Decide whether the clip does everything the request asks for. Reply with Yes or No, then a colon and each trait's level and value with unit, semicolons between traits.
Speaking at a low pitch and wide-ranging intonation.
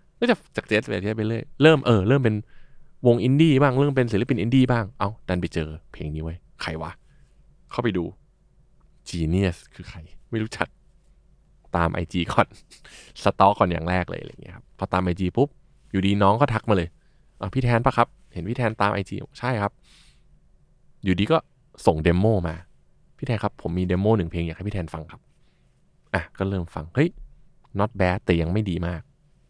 Yes: low, 100 Hz; wide, 6.1 semitones